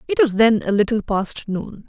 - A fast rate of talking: Yes, fast, 225 wpm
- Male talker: No, female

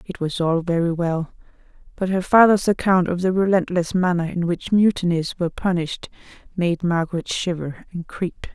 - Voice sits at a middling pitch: Yes, medium, 175 Hz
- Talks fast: No, average, 160 wpm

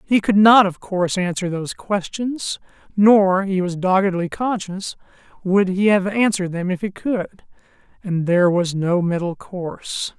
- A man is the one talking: Yes, male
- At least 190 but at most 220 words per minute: No, average, 155 wpm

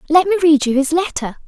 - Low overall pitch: No, very high, 315 Hz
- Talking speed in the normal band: No, fast, 245 wpm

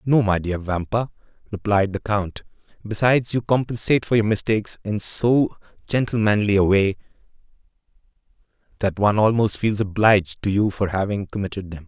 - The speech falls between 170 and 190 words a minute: No, average, 145 wpm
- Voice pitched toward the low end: Yes, low, 105 Hz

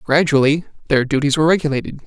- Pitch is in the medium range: Yes, medium, 145 Hz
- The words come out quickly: No, average, 145 wpm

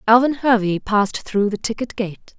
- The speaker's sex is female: Yes, female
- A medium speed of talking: Yes, average, 175 wpm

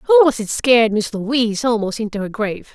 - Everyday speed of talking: No, fast, 220 wpm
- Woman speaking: Yes, female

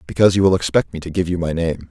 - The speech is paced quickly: Yes, fast, 315 wpm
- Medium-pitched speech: No, very low, 85 Hz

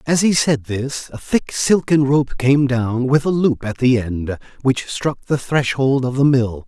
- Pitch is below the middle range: Yes, low, 130 Hz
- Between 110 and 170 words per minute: No, fast, 205 wpm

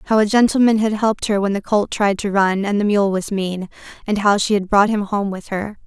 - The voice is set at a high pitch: Yes, high, 205 Hz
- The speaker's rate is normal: No, fast, 265 wpm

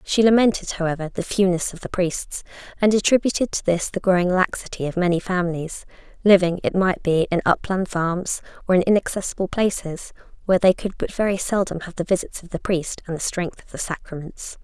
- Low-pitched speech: No, medium, 185 Hz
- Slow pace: No, average, 190 wpm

